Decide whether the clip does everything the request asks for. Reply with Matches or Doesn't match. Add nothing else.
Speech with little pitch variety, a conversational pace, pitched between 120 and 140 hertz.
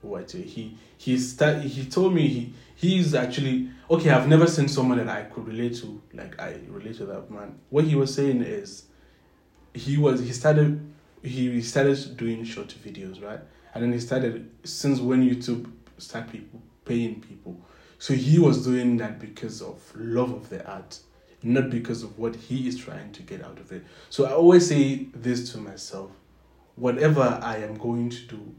Doesn't match